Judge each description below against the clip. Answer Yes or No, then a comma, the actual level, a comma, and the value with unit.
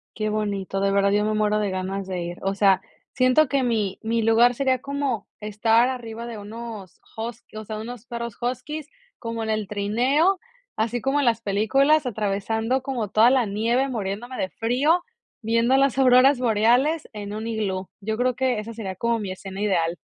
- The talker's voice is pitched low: No, high, 225 Hz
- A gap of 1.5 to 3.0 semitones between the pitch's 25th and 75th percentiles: No, average, 3.4 semitones